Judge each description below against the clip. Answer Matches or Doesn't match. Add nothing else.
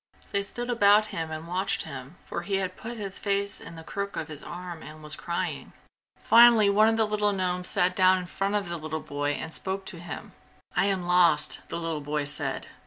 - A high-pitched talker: Doesn't match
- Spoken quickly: Matches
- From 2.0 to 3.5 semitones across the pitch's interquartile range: Doesn't match